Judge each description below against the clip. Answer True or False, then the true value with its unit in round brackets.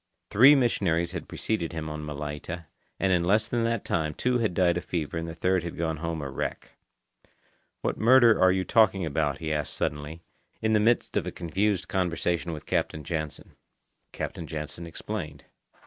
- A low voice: True (85 Hz)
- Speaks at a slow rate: False (180 wpm)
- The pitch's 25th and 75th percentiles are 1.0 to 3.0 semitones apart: False (4.1 semitones)